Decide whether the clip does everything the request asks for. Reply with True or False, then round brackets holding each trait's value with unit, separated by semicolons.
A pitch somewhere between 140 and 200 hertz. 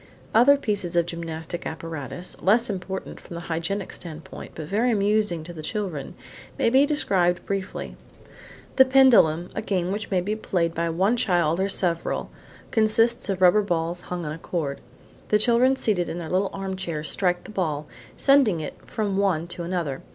True (185 Hz)